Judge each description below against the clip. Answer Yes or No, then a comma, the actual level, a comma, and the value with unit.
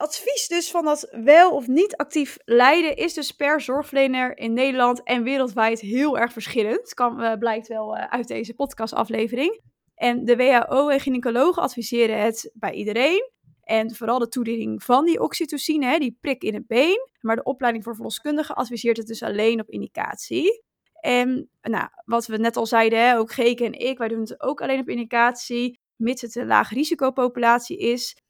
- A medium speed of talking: Yes, average, 180 wpm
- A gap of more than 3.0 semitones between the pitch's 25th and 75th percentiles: Yes, average, 3.8 semitones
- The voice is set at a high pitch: Yes, high, 245 Hz